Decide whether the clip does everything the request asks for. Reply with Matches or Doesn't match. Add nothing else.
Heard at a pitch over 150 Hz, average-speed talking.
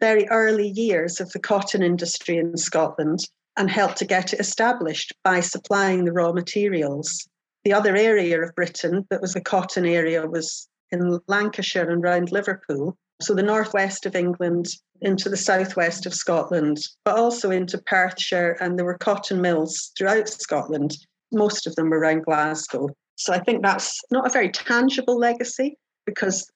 Matches